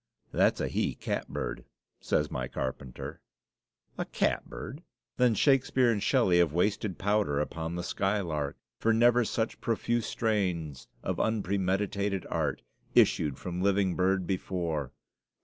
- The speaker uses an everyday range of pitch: Yes, average, 4.5 semitones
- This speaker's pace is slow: Yes, slow, 125 wpm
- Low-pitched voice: Yes, very low, 95 Hz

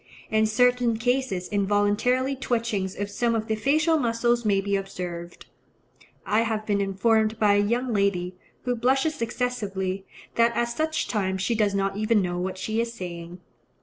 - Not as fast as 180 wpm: Yes, average, 165 wpm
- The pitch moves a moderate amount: Yes, average, 3.4 semitones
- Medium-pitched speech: No, high, 215 Hz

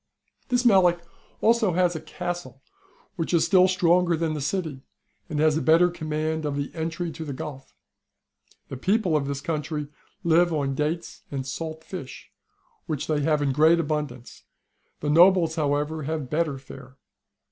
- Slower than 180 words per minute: Yes, average, 160 wpm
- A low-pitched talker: No, medium, 160 Hz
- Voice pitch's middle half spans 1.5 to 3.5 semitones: Yes, average, 2.9 semitones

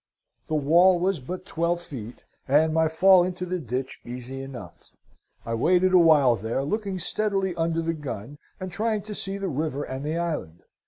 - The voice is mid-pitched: Yes, medium, 165 Hz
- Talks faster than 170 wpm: Yes, average, 180 wpm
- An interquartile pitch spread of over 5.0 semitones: Yes, wide, 5.4 semitones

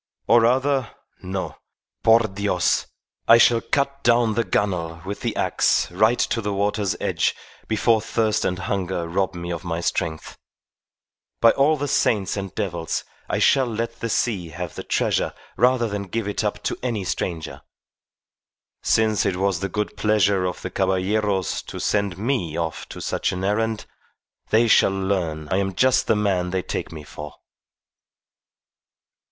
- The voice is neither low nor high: No, low, 100 Hz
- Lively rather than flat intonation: No, average, 3.7 semitones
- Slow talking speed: No, average, 160 wpm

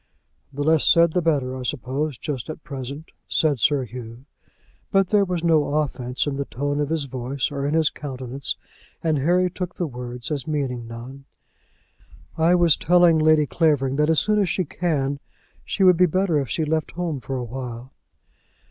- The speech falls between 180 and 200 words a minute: Yes, average, 185 wpm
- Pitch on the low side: No, medium, 145 Hz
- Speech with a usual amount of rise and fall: Yes, average, 3.8 semitones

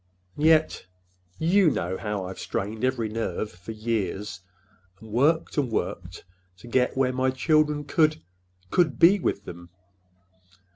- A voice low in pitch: Yes, low, 115 Hz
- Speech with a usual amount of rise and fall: No, wide, 8.1 semitones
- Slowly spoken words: Yes, slow, 130 wpm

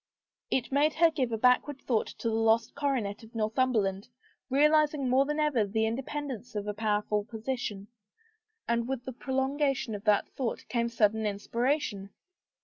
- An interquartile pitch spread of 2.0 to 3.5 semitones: No, average, 3.9 semitones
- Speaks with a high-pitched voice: Yes, high, 235 Hz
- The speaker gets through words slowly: No, average, 160 wpm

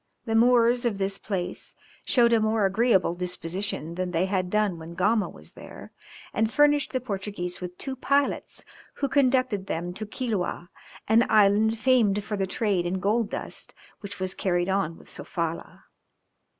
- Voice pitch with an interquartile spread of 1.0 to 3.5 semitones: No, average, 4.2 semitones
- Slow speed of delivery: No, average, 165 wpm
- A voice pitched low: No, high, 205 Hz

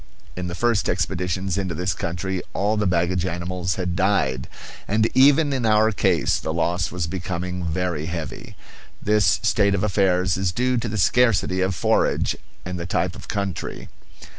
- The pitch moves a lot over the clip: No, average, 2.7 semitones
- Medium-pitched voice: No, very low, 90 Hz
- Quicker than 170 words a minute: No, average, 165 wpm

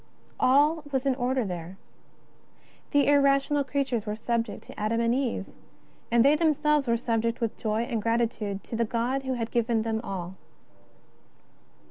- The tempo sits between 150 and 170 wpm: Yes, average, 155 wpm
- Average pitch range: Yes, average, 3.5 semitones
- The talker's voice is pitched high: Yes, high, 235 Hz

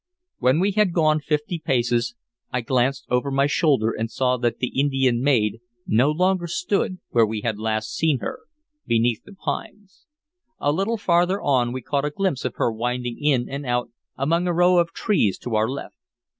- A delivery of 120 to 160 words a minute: No, average, 185 wpm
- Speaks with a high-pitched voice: No, low, 135 Hz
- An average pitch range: No, wide, 6.0 semitones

